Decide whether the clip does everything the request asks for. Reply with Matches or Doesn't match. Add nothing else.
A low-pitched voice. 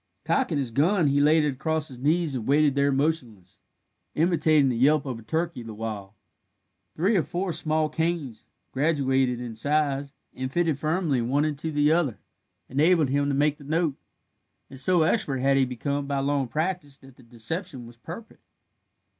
Doesn't match